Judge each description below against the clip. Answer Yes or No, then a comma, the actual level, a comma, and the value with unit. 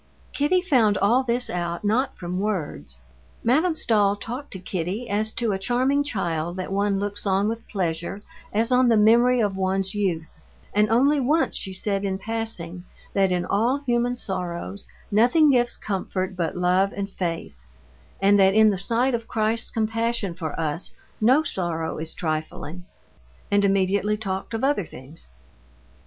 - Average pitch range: Yes, average, 4.2 semitones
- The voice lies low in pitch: No, high, 205 Hz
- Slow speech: No, average, 160 wpm